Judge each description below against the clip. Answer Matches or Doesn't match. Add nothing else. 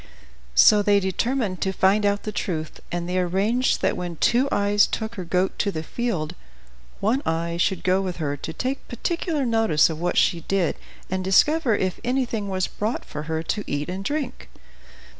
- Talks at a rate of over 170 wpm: Matches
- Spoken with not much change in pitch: Doesn't match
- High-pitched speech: Matches